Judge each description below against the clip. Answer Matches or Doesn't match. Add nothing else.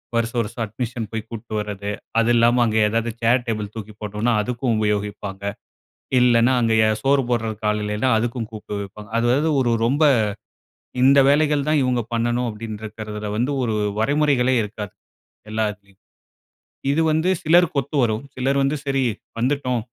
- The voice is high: Doesn't match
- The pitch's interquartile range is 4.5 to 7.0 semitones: Doesn't match